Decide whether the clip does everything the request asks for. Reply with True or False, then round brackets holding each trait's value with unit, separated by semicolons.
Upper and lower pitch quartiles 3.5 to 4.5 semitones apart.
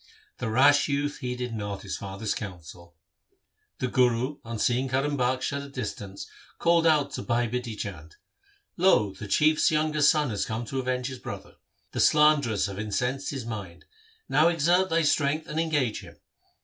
False (5.4 semitones)